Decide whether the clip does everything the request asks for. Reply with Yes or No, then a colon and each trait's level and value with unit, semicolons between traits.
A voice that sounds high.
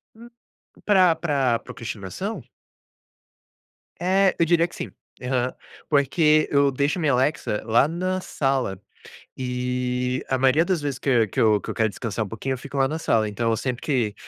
No: low, 135 Hz